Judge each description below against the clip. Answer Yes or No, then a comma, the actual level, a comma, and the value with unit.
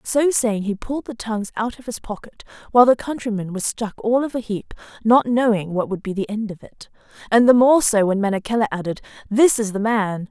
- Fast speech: Yes, fast, 225 wpm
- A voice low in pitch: No, high, 220 Hz